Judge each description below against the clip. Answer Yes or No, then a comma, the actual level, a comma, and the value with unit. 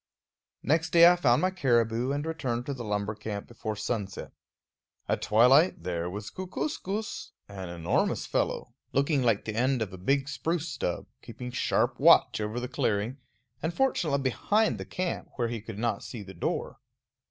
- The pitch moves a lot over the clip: Yes, wide, 6.0 semitones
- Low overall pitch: Yes, low, 120 Hz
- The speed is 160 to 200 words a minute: Yes, average, 170 wpm